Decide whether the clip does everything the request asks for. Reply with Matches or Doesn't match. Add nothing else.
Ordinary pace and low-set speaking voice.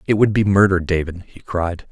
Doesn't match